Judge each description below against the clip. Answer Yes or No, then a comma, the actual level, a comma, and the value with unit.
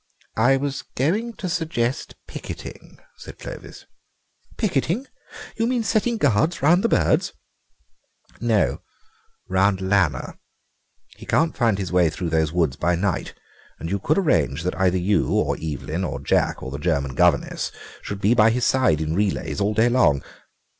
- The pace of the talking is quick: No, average, 155 wpm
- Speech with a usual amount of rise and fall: No, wide, 8.7 semitones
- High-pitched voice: No, low, 105 Hz